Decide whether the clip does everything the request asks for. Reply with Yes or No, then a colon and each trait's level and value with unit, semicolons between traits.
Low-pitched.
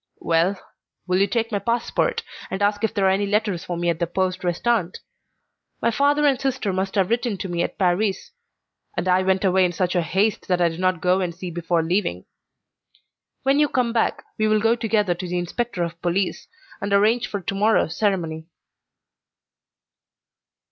No: high, 190 Hz